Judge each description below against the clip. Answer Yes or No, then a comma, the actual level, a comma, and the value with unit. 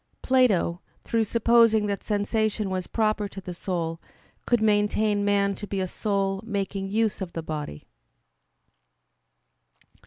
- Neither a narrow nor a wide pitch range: No, narrow, 2.3 semitones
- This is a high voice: Yes, high, 205 Hz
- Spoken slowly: Yes, slow, 130 wpm